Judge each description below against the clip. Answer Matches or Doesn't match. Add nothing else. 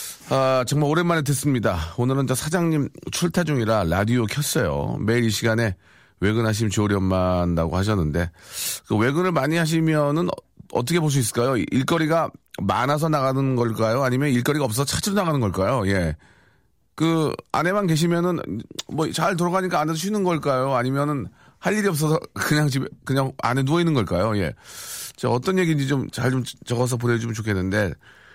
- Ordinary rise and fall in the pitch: Doesn't match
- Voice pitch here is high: Doesn't match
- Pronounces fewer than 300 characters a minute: Doesn't match